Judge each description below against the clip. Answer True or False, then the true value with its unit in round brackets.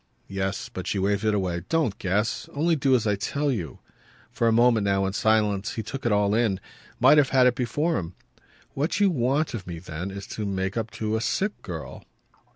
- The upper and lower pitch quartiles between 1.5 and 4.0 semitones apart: False (4.8 semitones)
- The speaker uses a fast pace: True (215 wpm)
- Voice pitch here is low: True (110 Hz)